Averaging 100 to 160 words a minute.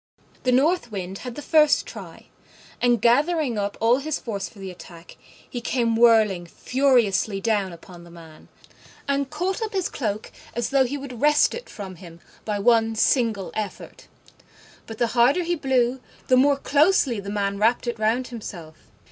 No: average, 175 wpm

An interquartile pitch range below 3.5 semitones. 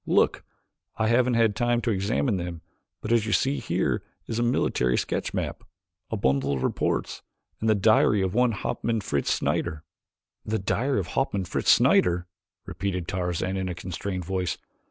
No: average, 4.3 semitones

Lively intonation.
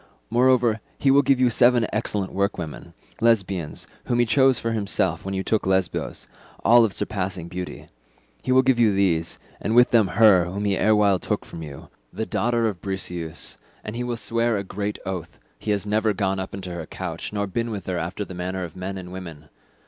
No: average, 3.8 semitones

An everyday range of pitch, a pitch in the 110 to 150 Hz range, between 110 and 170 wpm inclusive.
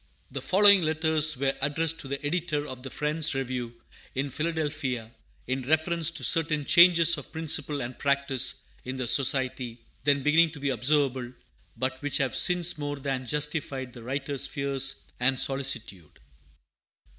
Yes: average, 3.1 semitones; medium, 140 Hz; average, 150 wpm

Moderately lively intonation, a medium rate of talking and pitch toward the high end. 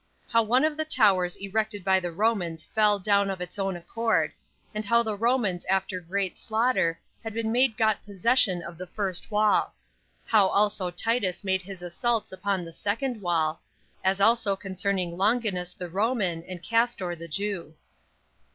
Yes: average, 3.6 semitones; average, 165 wpm; high, 200 Hz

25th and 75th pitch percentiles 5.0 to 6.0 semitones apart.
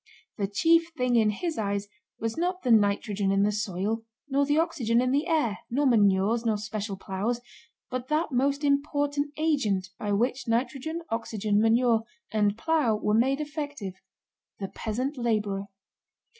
Yes: wide, 5.4 semitones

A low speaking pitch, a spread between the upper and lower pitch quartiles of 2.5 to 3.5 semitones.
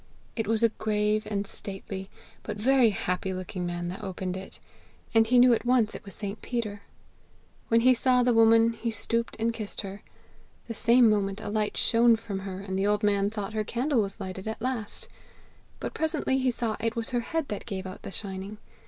No: high, 215 Hz; average, 2.8 semitones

